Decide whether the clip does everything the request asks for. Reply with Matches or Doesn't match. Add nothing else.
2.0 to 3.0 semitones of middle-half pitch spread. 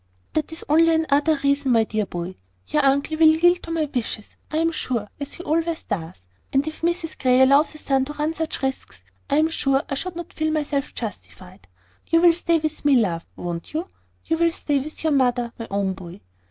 Doesn't match